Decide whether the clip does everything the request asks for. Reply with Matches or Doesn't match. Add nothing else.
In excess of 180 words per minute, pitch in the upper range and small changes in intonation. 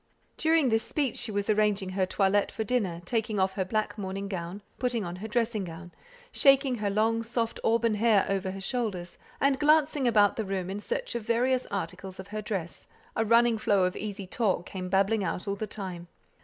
Doesn't match